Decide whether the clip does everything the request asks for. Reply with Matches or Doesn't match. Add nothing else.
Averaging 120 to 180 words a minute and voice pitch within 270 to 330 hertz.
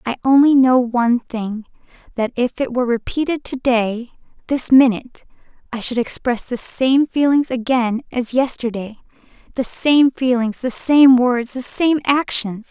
Doesn't match